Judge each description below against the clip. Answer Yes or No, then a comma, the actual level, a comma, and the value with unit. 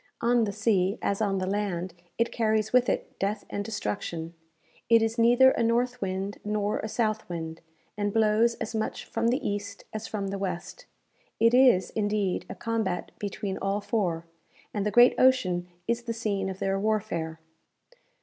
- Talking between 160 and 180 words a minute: Yes, average, 175 wpm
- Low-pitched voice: No, high, 210 Hz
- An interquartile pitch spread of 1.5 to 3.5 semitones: Yes, average, 2.9 semitones